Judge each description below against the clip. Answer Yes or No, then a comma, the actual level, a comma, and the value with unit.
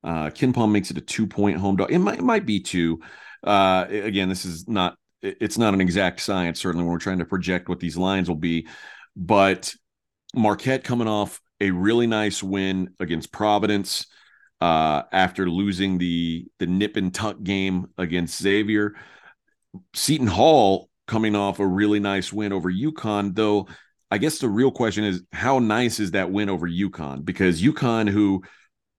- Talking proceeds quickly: No, average, 175 wpm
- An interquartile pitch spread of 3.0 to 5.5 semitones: No, narrow, 2.5 semitones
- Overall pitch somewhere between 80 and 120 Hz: Yes, very low, 95 Hz